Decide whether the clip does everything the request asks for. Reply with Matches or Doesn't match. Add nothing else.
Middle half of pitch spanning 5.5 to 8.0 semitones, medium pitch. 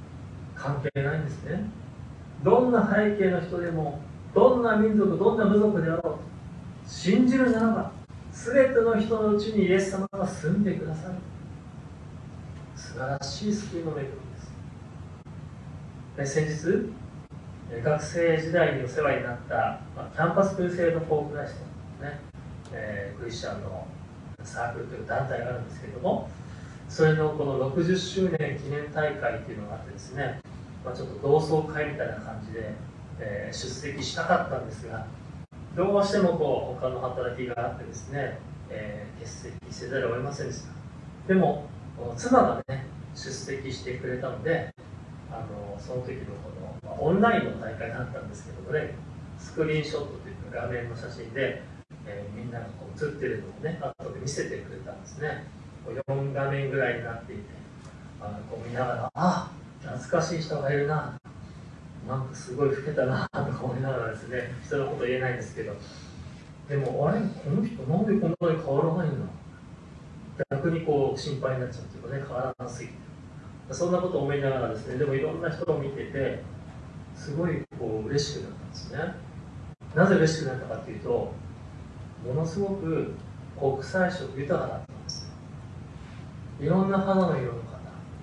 Doesn't match